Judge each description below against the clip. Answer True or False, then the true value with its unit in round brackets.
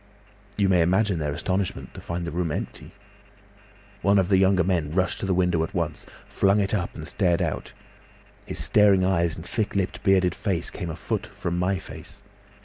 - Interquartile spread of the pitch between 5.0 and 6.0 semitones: False (2.4 semitones)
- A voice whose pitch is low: True (95 Hz)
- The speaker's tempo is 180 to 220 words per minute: True (195 wpm)